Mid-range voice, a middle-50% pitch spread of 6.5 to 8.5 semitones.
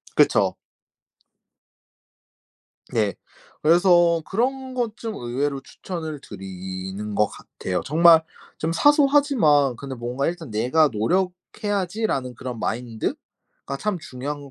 Yes: medium, 150 Hz; wide, 7.7 semitones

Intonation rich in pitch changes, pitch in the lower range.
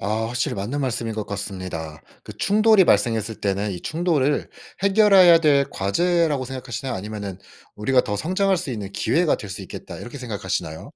Yes: wide, 8.1 semitones; low, 120 Hz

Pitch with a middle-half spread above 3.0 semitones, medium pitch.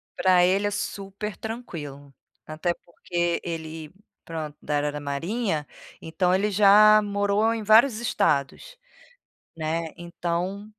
Yes: average, 4.6 semitones; medium, 180 Hz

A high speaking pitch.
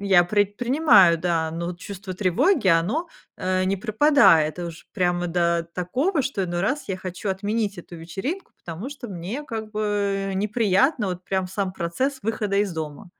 Yes: high, 195 Hz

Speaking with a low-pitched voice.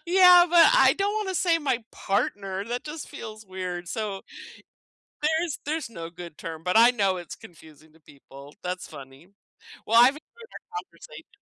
No: high, 215 Hz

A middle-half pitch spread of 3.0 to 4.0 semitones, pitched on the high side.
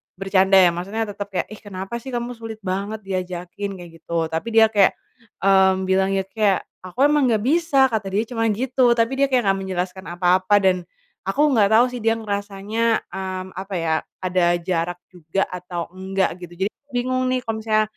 Yes: average, 3.4 semitones; high, 195 Hz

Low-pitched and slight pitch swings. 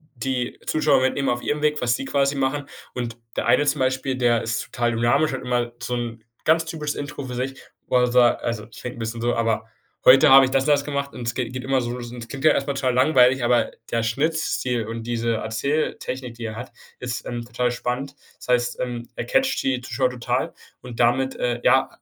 Yes: low, 125 Hz; narrow, 2.2 semitones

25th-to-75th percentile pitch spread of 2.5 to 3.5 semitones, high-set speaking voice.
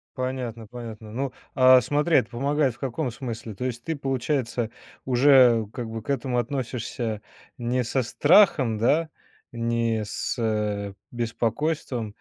No: average, 2.9 semitones; low, 120 Hz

